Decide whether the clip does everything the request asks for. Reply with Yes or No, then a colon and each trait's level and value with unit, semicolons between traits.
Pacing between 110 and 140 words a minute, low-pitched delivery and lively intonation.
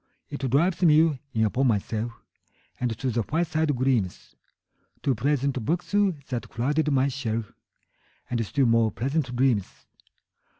No: slow, 135 wpm; low, 130 Hz; average, 4.3 semitones